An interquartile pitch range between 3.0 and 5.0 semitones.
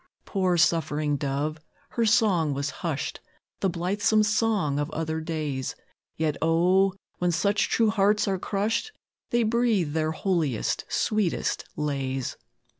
No: wide, 5.5 semitones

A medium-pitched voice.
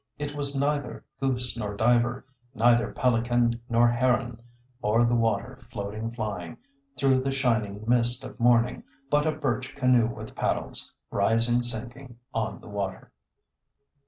No: low, 120 Hz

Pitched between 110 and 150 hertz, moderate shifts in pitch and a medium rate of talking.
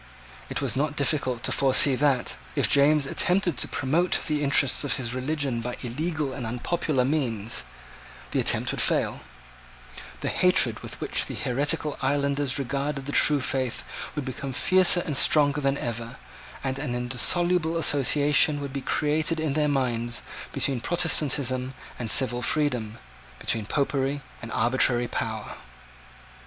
Yes: medium, 140 Hz; average, 3.0 semitones; average, 145 wpm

